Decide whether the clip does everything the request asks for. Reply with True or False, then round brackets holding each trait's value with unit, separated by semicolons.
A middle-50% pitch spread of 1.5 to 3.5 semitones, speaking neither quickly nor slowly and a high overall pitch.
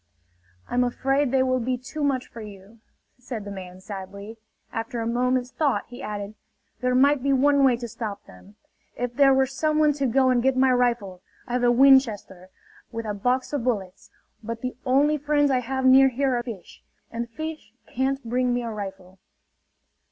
True (3.2 semitones; 190 wpm; 250 Hz)